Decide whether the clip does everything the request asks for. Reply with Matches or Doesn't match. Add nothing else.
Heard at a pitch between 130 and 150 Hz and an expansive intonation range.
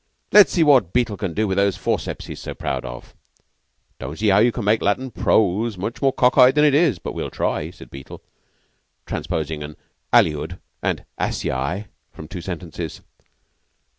Doesn't match